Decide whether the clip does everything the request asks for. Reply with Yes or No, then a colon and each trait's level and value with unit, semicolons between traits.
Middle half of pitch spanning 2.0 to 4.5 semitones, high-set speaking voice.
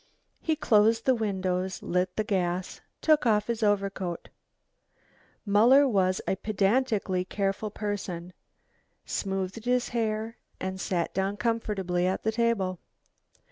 Yes: average, 3.2 semitones; high, 205 Hz